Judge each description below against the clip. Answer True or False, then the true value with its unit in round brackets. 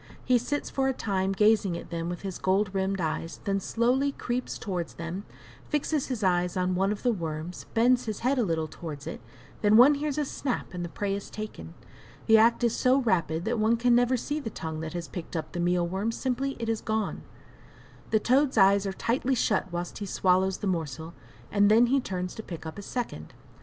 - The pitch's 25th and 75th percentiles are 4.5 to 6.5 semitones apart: True (5.4 semitones)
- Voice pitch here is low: False (200 Hz)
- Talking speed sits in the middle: False (220 wpm)